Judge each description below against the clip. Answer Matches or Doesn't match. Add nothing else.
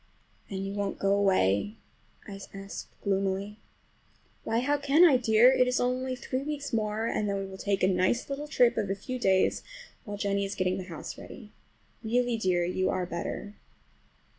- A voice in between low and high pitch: Doesn't match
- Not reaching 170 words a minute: Doesn't match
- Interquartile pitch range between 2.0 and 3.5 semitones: Doesn't match